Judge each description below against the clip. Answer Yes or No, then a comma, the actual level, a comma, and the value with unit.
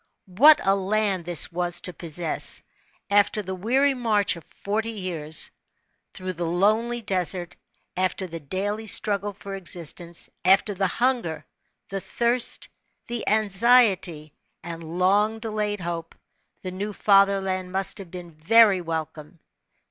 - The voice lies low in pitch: No, high, 190 Hz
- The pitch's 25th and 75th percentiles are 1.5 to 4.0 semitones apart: Yes, average, 3.3 semitones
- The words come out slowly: Yes, slow, 130 wpm